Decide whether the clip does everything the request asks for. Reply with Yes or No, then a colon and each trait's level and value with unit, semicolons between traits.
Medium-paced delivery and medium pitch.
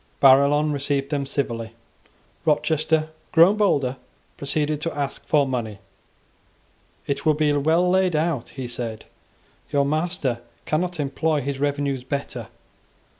No: slow, 125 wpm; medium, 145 Hz